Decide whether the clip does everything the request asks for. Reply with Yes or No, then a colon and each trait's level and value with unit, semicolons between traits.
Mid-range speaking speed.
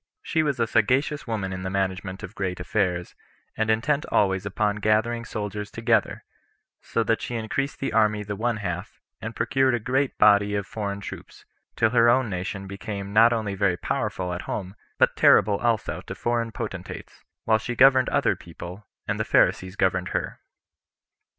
Yes: average, 175 wpm